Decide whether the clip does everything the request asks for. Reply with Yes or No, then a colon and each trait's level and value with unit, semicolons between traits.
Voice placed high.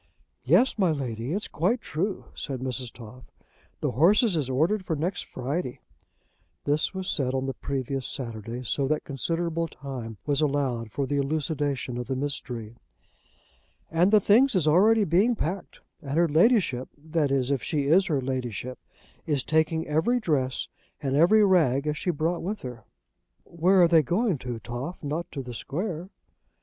No: medium, 150 Hz